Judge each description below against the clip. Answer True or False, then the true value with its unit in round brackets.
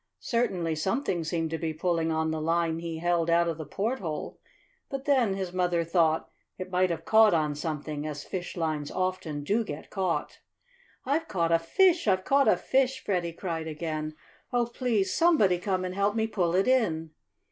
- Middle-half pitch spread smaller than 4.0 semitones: False (4.5 semitones)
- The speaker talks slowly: False (180 wpm)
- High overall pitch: False (175 Hz)